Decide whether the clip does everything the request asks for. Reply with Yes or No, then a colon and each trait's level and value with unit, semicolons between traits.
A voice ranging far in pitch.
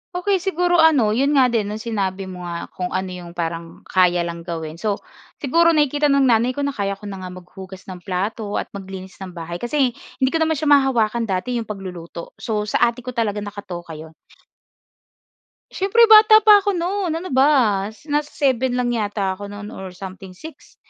Yes: wide, 7.2 semitones